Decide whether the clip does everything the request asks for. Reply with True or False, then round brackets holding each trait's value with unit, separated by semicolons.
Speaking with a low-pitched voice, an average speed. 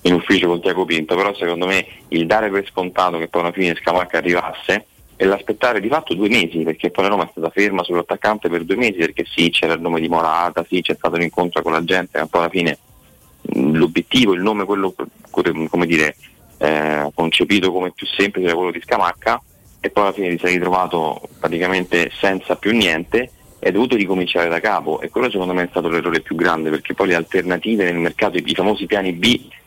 False (90 Hz; 210 wpm)